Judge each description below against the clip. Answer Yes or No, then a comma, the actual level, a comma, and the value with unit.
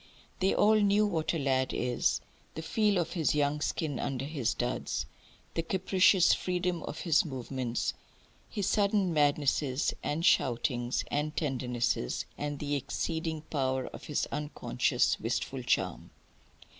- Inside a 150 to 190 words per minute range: No, slow, 135 wpm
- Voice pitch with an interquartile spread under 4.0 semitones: No, average, 4.9 semitones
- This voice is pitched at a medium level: Yes, medium, 150 Hz